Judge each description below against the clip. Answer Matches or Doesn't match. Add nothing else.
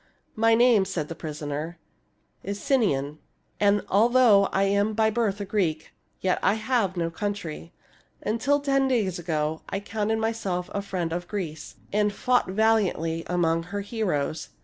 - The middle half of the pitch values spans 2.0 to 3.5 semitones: Doesn't match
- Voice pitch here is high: Matches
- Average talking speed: Matches